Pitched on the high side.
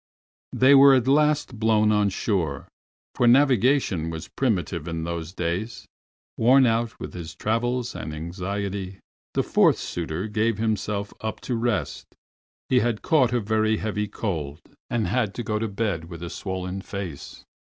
No: low, 105 Hz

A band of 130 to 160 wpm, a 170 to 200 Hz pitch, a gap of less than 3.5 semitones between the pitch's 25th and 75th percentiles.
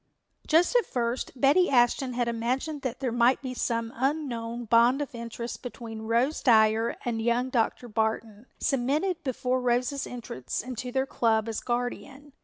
No: average, 155 wpm; high, 245 Hz; narrow, 2.4 semitones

